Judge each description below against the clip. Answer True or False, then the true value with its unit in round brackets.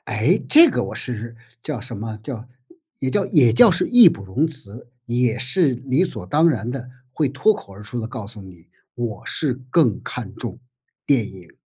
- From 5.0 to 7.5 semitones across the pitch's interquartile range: True (5.3 semitones)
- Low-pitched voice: True (125 Hz)